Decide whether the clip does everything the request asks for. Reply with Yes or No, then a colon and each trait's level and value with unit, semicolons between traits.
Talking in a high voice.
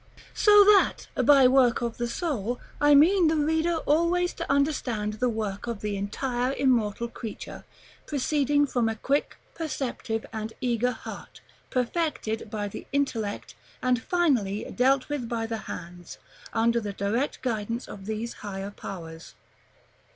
Yes: high, 240 Hz